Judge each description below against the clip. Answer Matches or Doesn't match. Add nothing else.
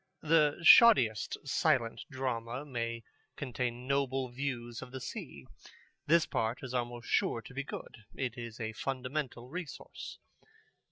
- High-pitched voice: Doesn't match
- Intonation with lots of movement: Doesn't match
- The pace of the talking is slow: Matches